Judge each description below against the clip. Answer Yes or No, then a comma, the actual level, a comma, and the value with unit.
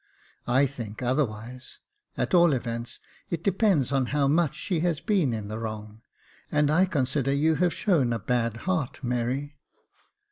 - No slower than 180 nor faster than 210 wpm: No, average, 165 wpm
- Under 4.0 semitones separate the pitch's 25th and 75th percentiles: No, average, 5.2 semitones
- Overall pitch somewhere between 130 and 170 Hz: Yes, low, 135 Hz